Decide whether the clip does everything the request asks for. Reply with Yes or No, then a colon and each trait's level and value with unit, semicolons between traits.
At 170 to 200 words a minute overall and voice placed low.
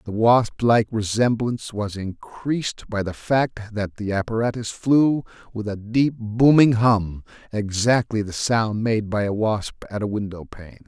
No: average, 155 wpm; low, 110 Hz